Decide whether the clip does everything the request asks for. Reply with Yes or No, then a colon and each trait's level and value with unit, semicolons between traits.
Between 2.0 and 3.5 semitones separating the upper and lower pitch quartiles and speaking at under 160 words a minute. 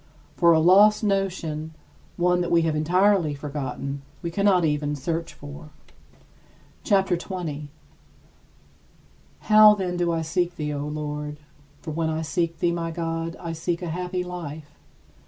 Yes: average, 2.8 semitones; average, 150 wpm